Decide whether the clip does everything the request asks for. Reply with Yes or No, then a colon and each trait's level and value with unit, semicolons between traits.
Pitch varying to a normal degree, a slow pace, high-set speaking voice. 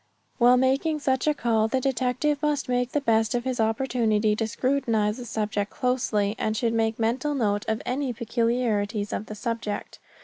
No: average, 3.0 semitones; average, 175 wpm; high, 235 Hz